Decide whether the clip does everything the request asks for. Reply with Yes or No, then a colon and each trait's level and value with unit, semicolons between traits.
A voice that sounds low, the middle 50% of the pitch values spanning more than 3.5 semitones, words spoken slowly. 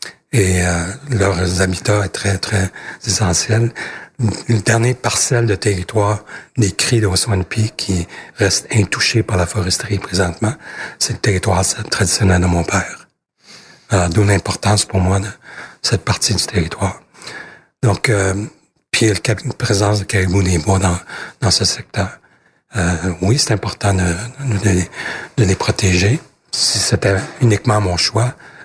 No: low, 100 Hz; average, 2.8 semitones; slow, 140 wpm